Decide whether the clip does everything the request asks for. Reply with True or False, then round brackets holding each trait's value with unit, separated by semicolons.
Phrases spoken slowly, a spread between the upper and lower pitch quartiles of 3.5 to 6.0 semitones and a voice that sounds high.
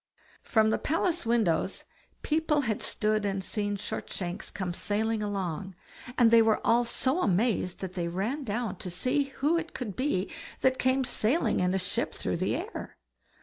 False (170 wpm; 5.2 semitones; 220 Hz)